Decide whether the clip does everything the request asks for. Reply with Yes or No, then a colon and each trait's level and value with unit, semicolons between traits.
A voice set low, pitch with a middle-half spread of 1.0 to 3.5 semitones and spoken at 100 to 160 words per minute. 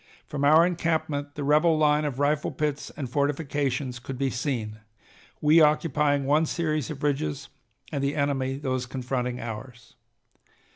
No: medium, 145 Hz; narrow, 2.6 semitones; average, 145 wpm